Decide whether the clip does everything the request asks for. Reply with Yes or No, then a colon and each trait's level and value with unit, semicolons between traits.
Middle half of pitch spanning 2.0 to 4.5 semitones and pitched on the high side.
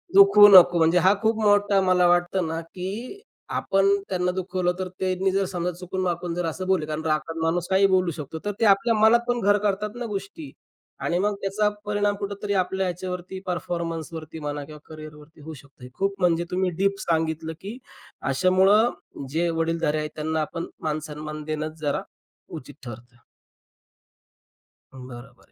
No: average, 3.6 semitones; medium, 180 Hz